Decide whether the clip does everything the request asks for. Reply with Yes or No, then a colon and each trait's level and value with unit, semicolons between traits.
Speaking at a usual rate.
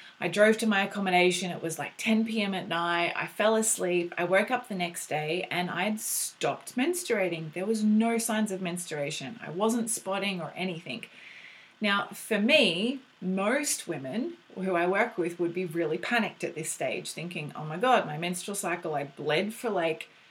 Yes: average, 185 wpm